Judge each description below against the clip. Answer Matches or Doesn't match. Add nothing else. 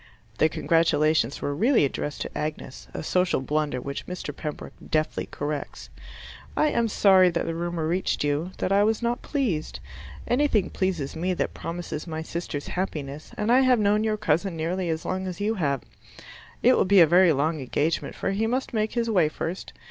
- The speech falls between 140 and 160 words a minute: Doesn't match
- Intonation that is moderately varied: Matches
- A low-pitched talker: Doesn't match